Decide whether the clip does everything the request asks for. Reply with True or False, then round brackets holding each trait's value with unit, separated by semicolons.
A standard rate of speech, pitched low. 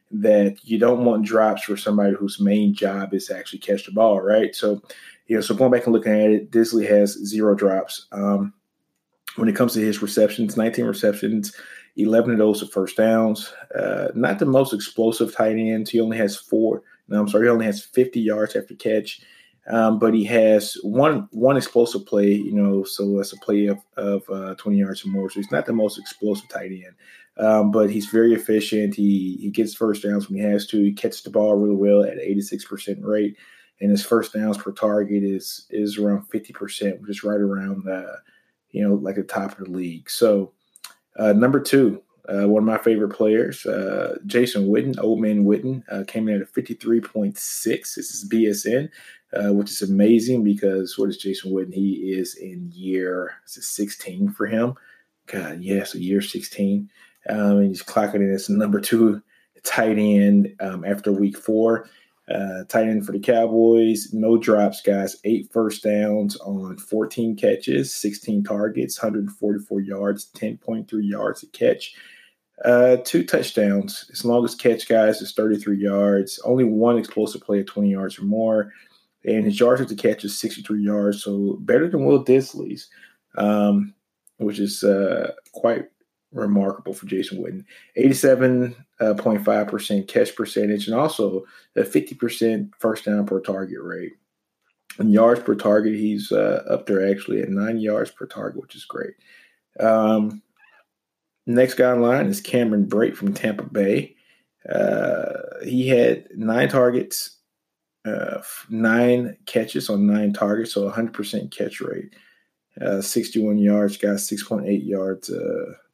True (180 wpm; 105 Hz)